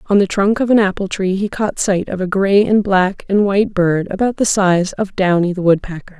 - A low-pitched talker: No, high, 195 Hz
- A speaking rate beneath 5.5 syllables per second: Yes, 5.2 syllables/s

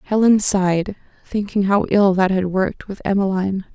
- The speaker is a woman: Yes, female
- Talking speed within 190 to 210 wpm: No, average, 160 wpm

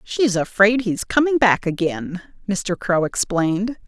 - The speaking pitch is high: Yes, high, 200 Hz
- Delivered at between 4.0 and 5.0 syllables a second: Yes, 4.1 syllables/s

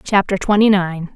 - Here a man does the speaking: No, female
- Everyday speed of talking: Yes, average, 155 wpm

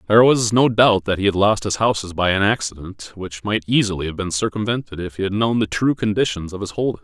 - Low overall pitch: Yes, low, 105 Hz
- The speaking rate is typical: No, fast, 245 wpm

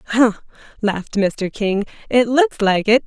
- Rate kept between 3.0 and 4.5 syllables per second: Yes, 4.2 syllables/s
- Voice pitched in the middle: No, high, 220 Hz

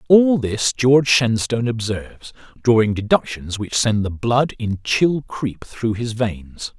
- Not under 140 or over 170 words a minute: Yes, average, 150 wpm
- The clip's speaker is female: No, male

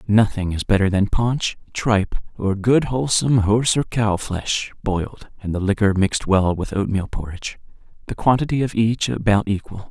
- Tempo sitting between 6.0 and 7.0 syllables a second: No, 5.2 syllables/s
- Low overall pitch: Yes, low, 105 Hz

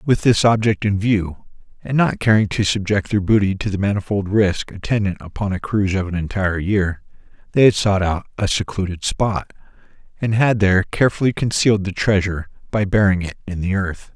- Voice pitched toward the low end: Yes, low, 100 Hz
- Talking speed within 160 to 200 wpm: Yes, average, 185 wpm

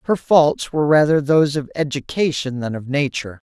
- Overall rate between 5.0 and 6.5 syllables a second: Yes, 5.6 syllables/s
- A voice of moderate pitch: Yes, medium, 145 Hz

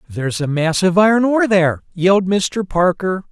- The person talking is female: No, male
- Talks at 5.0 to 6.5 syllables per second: Yes, 5.3 syllables/s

